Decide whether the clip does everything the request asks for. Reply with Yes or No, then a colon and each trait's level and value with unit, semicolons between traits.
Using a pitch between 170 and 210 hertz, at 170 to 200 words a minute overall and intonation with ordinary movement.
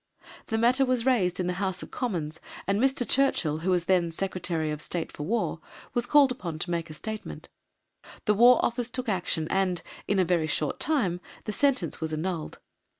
No: high, 190 Hz; average, 195 wpm; wide, 6.1 semitones